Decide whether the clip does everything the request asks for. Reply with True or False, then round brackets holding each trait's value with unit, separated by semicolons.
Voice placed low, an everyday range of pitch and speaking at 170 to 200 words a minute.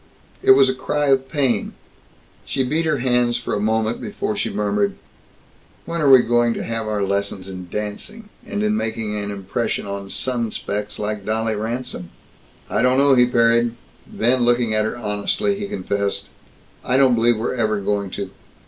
True (115 Hz; 3.7 semitones; 180 wpm)